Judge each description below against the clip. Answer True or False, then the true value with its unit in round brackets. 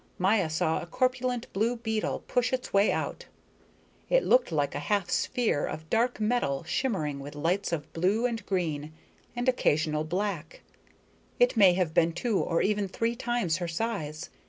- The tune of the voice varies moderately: False (6.6 semitones)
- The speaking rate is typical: True (165 wpm)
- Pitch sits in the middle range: False (195 Hz)